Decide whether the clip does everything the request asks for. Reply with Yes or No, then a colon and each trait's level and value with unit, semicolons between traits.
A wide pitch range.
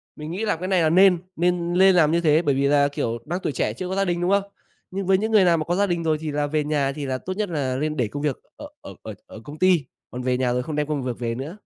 No: average, 4.3 semitones